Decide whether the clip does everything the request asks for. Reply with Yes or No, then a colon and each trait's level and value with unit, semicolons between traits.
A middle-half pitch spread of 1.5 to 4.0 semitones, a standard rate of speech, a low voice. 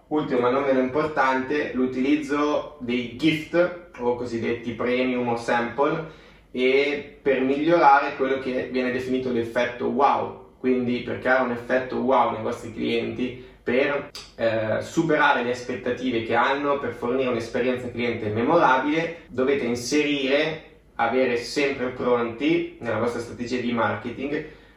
Yes: average, 2.9 semitones; average, 130 wpm; low, 130 Hz